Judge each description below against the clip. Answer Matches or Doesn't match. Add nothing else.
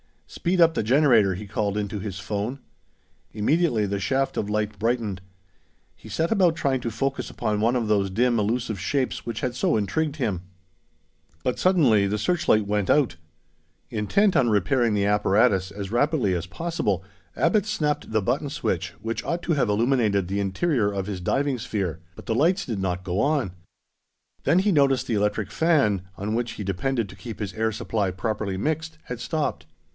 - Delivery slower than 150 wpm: Doesn't match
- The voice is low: Matches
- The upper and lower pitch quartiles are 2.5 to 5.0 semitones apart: Doesn't match